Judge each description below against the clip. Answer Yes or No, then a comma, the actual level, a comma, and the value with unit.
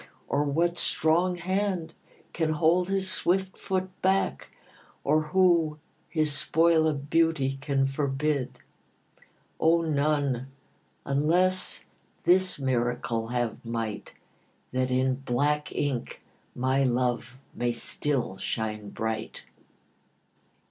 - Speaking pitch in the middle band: Yes, medium, 145 Hz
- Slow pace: Yes, slow, 100 wpm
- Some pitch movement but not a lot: Yes, average, 4.8 semitones